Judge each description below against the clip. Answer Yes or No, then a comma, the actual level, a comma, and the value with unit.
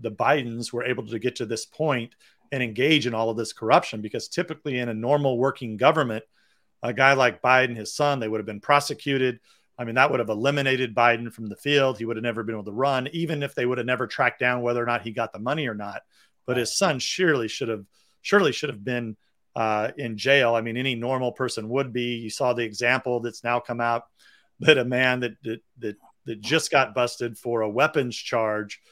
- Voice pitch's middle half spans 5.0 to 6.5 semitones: No, average, 2.7 semitones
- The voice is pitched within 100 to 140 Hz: Yes, low, 120 Hz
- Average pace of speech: No, fast, 230 wpm